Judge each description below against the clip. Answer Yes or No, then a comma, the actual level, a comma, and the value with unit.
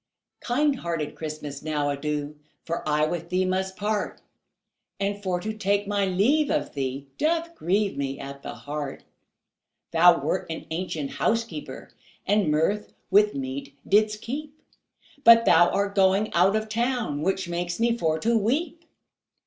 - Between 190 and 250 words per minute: No, average, 150 wpm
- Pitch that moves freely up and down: Yes, wide, 5.9 semitones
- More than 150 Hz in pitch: Yes, high, 190 Hz